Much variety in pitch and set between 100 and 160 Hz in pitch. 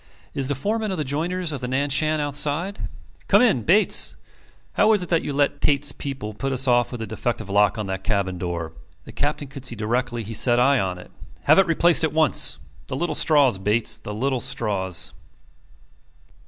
Yes: wide, 5.7 semitones; low, 135 Hz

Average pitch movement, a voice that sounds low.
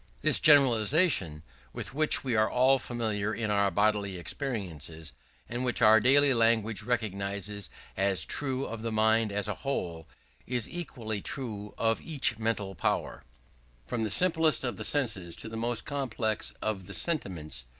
Yes: average, 4.1 semitones; low, 110 Hz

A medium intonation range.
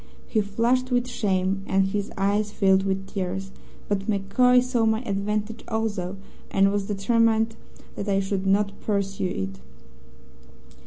No: narrow, 2.3 semitones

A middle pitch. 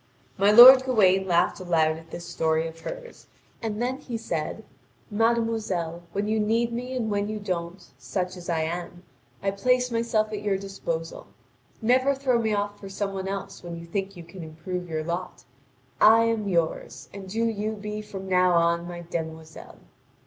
No: high, 195 Hz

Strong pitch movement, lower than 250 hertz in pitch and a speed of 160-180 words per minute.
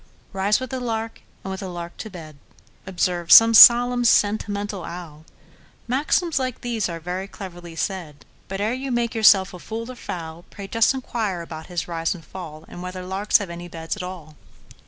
No: average, 4.7 semitones; high, 190 Hz; average, 170 wpm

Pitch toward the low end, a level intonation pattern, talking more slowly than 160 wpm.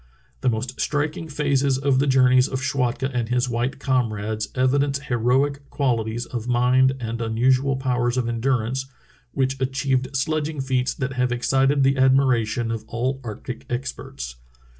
Yes: low, 130 Hz; narrow, 2.1 semitones; average, 145 wpm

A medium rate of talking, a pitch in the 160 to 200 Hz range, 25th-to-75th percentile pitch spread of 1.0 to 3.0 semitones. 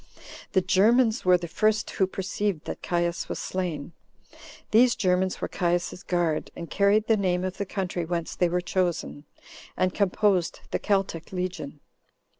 Yes: average, 155 wpm; medium, 185 Hz; narrow, 2.4 semitones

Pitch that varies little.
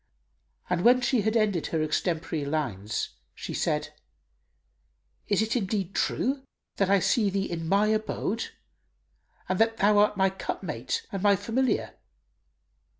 No: average, 3.8 semitones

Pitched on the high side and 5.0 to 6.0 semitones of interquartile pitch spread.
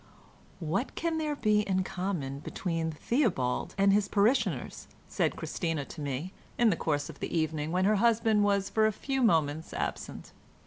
Yes: high, 195 Hz; average, 5.3 semitones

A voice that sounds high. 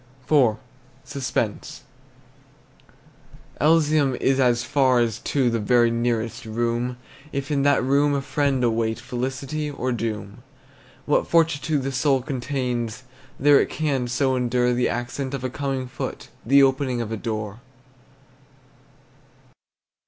No: low, 130 Hz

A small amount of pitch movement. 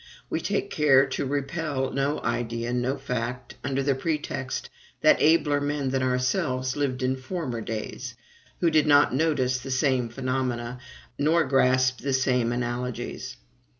Yes: narrow, 2.1 semitones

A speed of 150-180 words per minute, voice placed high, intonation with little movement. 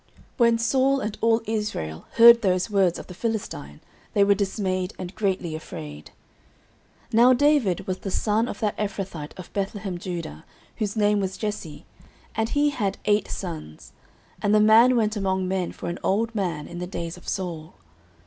No: average, 175 wpm; high, 200 Hz; average, 3.6 semitones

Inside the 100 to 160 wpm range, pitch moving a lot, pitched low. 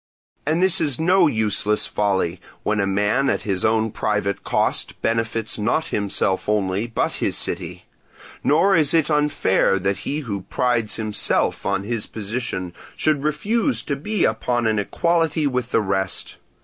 Yes: average, 155 wpm; wide, 6.5 semitones; low, 115 Hz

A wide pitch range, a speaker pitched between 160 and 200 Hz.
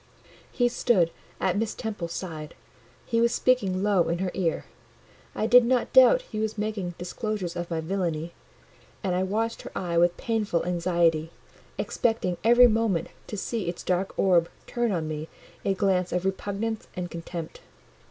No: average, 4.3 semitones; high, 190 Hz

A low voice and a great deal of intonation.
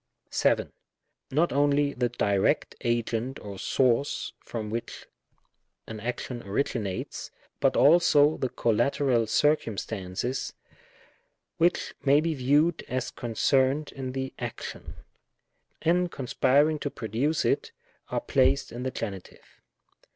No: low, 130 Hz; average, 4.0 semitones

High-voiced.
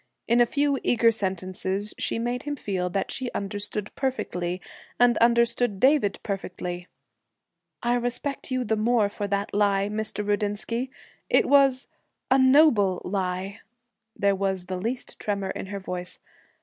Yes: high, 210 Hz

